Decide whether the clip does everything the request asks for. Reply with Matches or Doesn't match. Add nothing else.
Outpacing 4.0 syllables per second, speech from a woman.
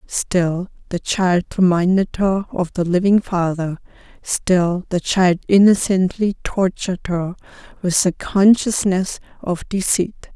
Doesn't match